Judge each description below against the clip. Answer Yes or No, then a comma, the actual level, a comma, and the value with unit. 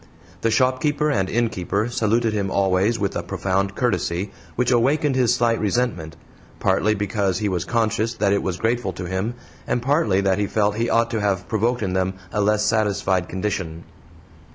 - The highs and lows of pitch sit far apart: No, average, 3.6 semitones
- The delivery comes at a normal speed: Yes, average, 175 wpm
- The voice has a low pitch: Yes, low, 105 Hz